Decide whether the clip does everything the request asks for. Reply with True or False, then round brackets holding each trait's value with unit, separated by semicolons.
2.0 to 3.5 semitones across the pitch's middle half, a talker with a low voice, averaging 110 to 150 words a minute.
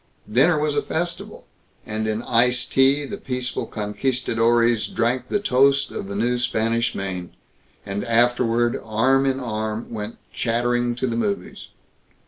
True (2.8 semitones; 120 Hz; 140 wpm)